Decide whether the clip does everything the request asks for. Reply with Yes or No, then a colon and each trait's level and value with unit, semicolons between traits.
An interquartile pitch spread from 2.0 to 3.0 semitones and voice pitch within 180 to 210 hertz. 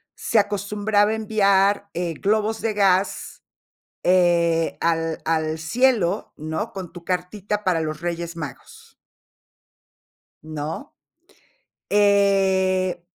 No: average, 3.5 semitones; medium, 185 Hz